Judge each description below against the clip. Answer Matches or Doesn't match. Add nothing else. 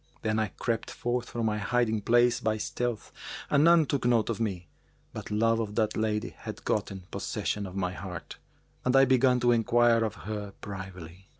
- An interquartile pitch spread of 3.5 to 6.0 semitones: Doesn't match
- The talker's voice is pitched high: Doesn't match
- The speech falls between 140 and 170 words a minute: Doesn't match